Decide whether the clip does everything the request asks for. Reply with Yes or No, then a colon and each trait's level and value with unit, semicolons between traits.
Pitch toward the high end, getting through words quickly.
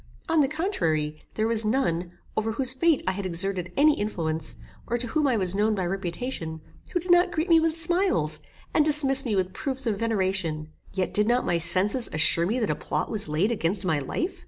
Yes: high, 215 Hz; fast, 210 wpm